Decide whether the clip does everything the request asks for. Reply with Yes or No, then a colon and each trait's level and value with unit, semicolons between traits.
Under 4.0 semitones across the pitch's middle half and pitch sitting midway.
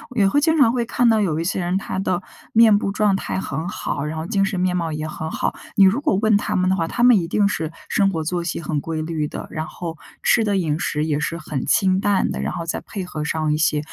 No: average, 4.3 semitones; medium, 180 Hz